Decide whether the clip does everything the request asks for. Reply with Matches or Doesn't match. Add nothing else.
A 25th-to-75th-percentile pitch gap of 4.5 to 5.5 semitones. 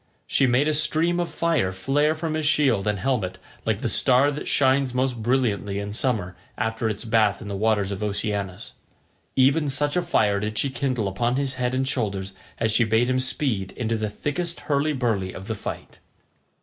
Matches